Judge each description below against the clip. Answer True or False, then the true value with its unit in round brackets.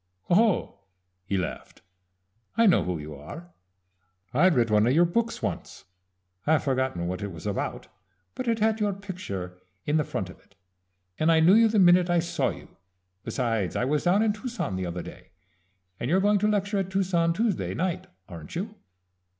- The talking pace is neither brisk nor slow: True (185 wpm)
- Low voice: False (170 Hz)